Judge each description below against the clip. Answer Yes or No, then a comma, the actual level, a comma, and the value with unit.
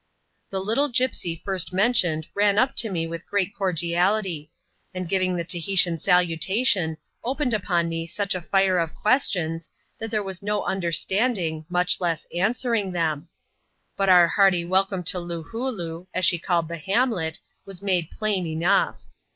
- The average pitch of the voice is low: No, medium, 185 Hz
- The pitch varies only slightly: No, average, 3.3 semitones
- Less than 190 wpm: Yes, average, 150 wpm